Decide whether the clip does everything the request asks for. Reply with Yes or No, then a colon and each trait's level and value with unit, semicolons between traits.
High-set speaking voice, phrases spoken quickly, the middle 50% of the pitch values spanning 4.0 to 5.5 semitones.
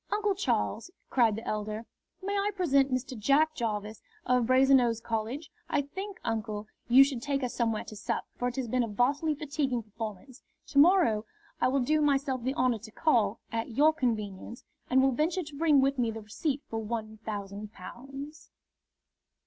No: very high, 250 Hz; average, 180 wpm; average, 4.3 semitones